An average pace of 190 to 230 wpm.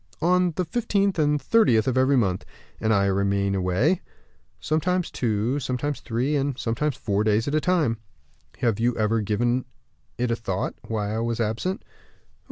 No: average, 165 wpm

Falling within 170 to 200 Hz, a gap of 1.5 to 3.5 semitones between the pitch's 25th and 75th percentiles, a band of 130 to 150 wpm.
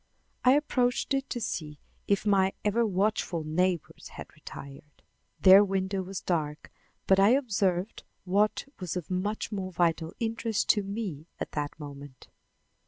No: high, 190 Hz; average, 4.1 semitones; average, 145 wpm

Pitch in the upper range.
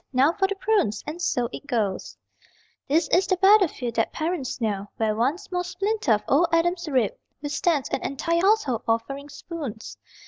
Yes: very high, 295 Hz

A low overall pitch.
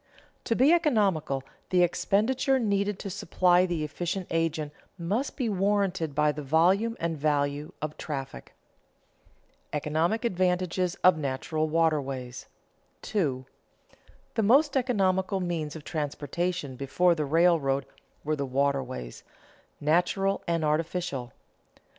No: medium, 170 Hz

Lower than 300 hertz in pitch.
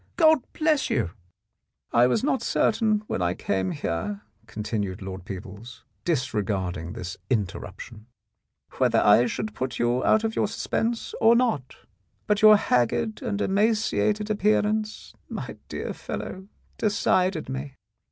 Yes: medium, 140 Hz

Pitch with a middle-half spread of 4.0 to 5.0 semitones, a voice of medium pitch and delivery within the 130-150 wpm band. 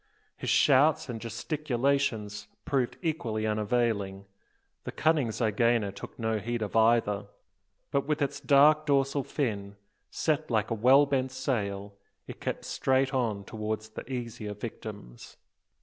No: average, 4.4 semitones; low, 115 Hz; slow, 135 wpm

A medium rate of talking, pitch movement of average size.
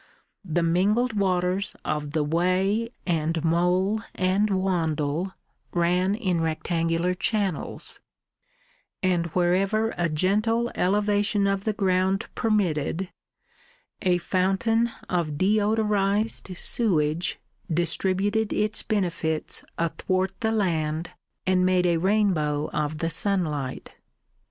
No: slow, 100 wpm; average, 3.5 semitones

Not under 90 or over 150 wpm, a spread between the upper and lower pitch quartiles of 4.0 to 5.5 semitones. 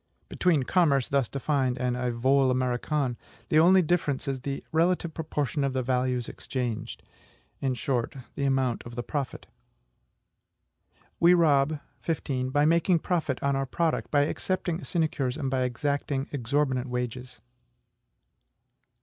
No: average, 140 wpm; average, 3.4 semitones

